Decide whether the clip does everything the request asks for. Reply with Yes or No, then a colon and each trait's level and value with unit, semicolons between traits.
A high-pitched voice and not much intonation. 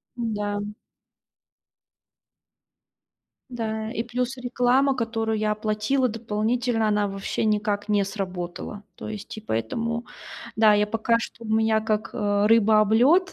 Yes: high, 220 Hz; narrow, 1.9 semitones